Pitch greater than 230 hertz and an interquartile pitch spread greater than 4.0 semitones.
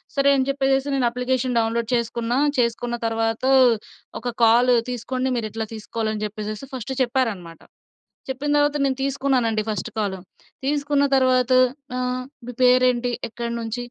No: high, 245 Hz; average, 2.7 semitones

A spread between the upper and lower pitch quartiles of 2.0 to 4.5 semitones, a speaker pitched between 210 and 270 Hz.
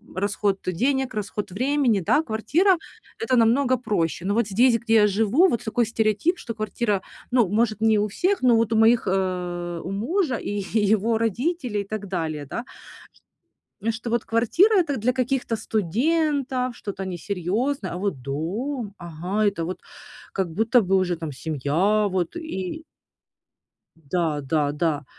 No: average, 5.0 semitones; high, 215 Hz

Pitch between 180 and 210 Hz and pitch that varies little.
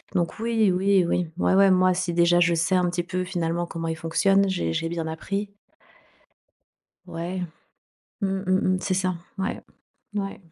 Yes: medium, 185 Hz; narrow, 2.1 semitones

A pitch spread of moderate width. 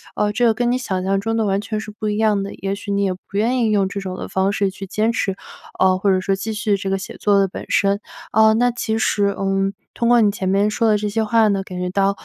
No: narrow, 2.0 semitones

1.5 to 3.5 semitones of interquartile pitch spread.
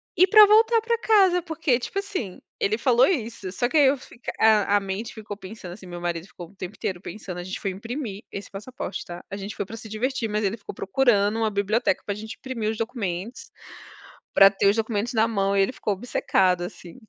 No: average, 4.2 semitones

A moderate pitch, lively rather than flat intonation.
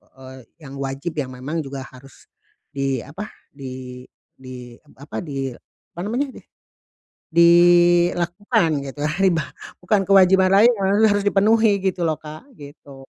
Yes: medium, 165 Hz; wide, 6.0 semitones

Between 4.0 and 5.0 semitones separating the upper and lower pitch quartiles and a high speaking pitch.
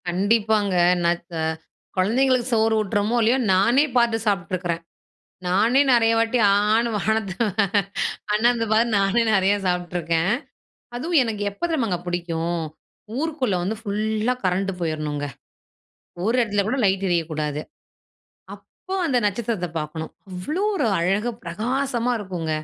Yes: average, 4.7 semitones; high, 205 Hz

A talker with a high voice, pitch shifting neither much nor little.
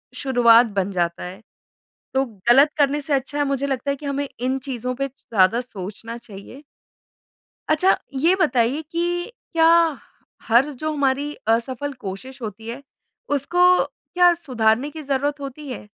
Yes: very high, 270 Hz; average, 3.8 semitones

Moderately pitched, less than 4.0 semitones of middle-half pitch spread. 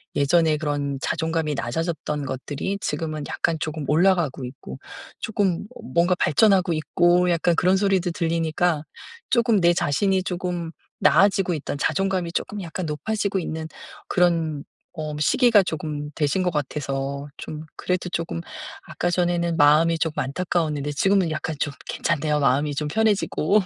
Yes: medium, 165 Hz; average, 3.4 semitones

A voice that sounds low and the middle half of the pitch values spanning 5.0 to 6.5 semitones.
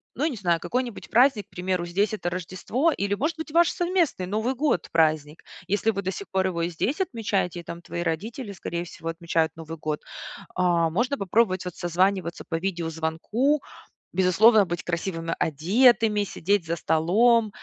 No: medium, 185 Hz; average, 5.3 semitones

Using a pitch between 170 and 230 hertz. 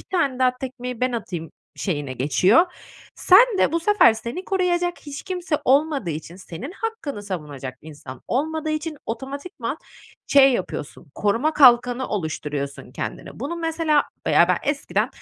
No: very high, 260 Hz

